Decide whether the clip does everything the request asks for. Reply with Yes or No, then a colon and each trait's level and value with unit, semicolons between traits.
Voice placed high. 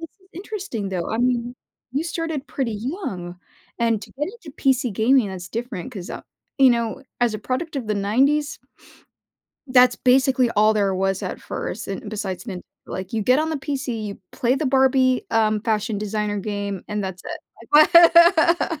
Yes: high, 240 Hz